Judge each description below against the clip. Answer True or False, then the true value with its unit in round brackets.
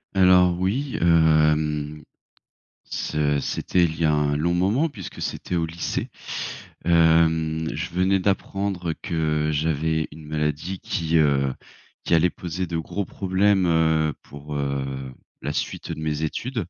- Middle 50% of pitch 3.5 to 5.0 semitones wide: False (3.0 semitones)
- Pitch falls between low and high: False (80 Hz)